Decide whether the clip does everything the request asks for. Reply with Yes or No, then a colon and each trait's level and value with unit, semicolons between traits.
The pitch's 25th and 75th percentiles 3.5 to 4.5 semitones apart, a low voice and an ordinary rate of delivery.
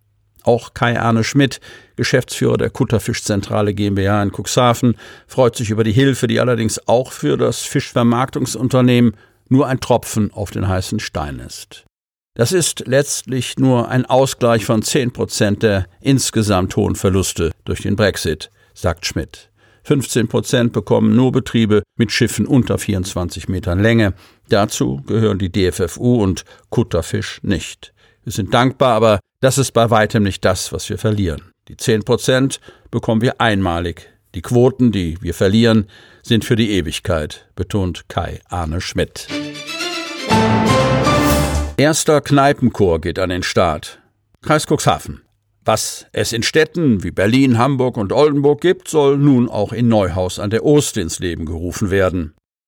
Yes: average, 4.2 semitones; low, 110 Hz; average, 145 wpm